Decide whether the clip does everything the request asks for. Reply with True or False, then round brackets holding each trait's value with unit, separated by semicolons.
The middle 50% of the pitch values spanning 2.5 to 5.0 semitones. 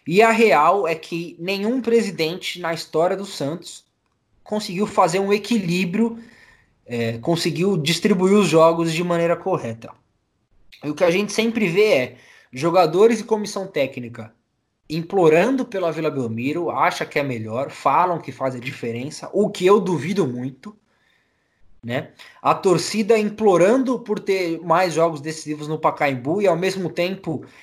False (5.4 semitones)